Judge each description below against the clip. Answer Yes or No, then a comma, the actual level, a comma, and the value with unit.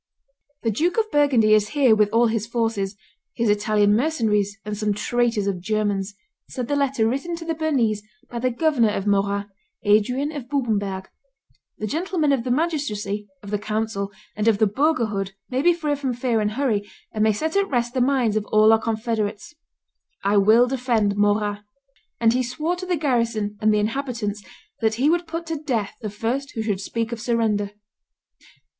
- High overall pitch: Yes, high, 225 Hz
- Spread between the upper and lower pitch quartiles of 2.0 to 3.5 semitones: No, average, 4.6 semitones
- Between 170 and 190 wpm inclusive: Yes, average, 185 wpm